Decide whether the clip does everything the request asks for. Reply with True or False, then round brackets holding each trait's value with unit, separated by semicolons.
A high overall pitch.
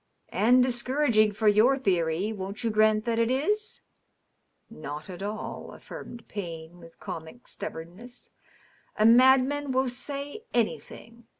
True (230 Hz)